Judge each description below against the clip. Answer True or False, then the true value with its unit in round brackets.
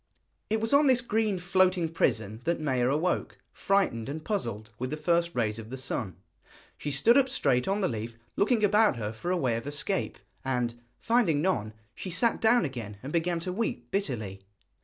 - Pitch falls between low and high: True (155 Hz)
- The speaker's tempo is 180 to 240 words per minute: True (190 wpm)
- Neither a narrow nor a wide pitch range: False (8.7 semitones)